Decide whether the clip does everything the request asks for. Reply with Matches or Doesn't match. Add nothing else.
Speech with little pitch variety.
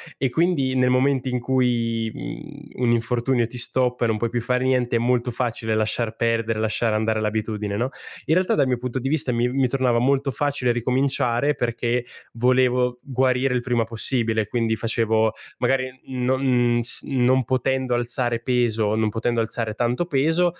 Matches